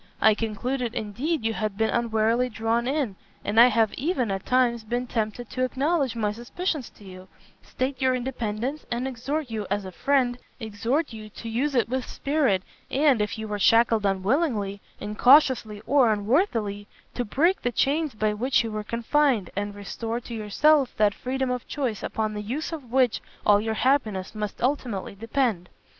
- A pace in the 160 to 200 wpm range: Yes, average, 175 wpm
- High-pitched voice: Yes, high, 230 Hz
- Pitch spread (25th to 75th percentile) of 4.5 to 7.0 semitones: No, average, 3.8 semitones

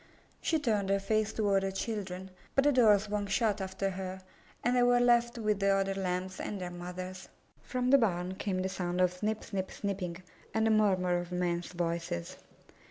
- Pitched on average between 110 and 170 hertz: No, high, 195 Hz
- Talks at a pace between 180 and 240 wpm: Yes, average, 190 wpm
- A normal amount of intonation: Yes, average, 3.0 semitones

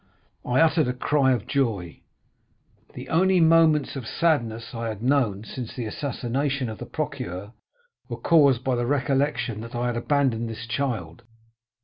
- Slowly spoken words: No, average, 155 wpm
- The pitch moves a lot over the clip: No, average, 3.8 semitones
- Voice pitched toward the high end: No, low, 125 Hz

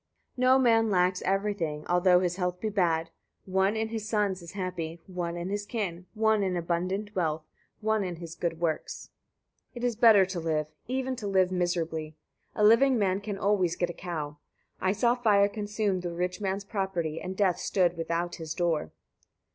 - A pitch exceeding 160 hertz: Yes, medium, 185 Hz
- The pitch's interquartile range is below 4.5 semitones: Yes, average, 3.4 semitones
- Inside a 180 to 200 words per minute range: Yes, average, 185 wpm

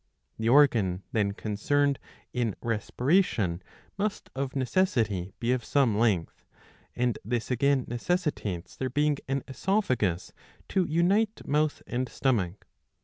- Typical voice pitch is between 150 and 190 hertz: No, low, 125 Hz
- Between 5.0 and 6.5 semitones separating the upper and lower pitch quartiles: Yes, average, 5.3 semitones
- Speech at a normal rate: No, slow, 120 wpm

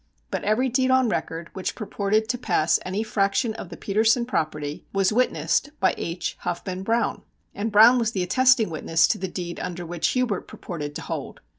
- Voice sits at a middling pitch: No, high, 200 Hz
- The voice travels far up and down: No, average, 5.0 semitones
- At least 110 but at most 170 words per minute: No, average, 185 wpm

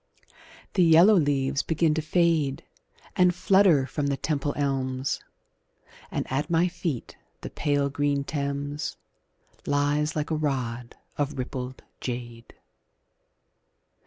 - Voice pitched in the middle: Yes, medium, 145 Hz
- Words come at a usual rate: No, slow, 115 wpm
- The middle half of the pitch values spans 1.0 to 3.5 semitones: Yes, average, 2.8 semitones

